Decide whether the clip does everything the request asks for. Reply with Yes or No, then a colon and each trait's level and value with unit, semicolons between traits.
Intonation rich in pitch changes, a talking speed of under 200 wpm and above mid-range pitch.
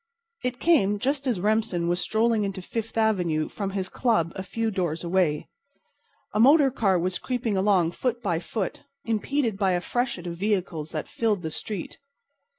No: average, 4.3 semitones; average, 170 wpm; high, 200 Hz